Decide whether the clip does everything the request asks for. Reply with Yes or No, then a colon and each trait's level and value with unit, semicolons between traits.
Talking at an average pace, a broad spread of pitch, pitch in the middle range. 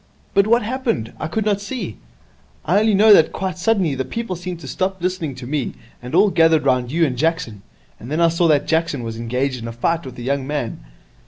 No: fast, 230 wpm; wide, 6.7 semitones; medium, 160 Hz